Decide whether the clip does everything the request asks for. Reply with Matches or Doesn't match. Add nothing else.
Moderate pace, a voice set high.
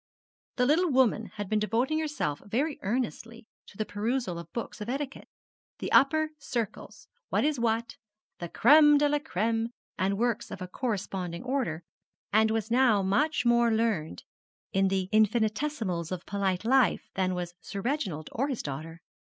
Matches